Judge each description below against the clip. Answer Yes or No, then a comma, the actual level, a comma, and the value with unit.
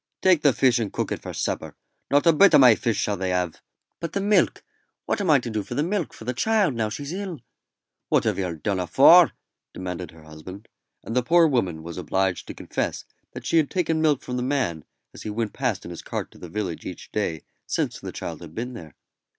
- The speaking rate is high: Yes, fast, 235 wpm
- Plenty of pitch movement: Yes, wide, 8.7 semitones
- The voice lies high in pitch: No, low, 115 Hz